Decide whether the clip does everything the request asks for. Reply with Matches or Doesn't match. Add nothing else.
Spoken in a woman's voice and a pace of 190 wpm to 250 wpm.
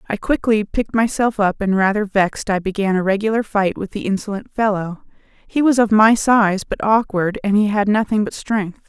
Matches